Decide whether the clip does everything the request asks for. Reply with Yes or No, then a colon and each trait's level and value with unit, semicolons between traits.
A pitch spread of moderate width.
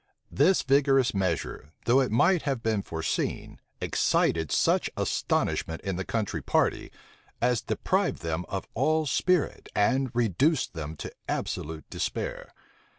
No: wide, 7.6 semitones